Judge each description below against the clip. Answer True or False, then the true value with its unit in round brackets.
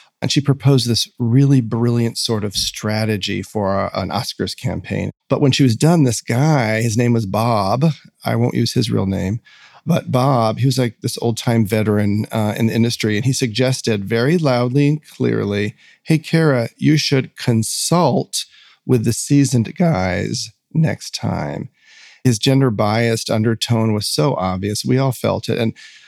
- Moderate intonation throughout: True (3.8 semitones)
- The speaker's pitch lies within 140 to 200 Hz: False (115 Hz)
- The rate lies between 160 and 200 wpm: True (170 wpm)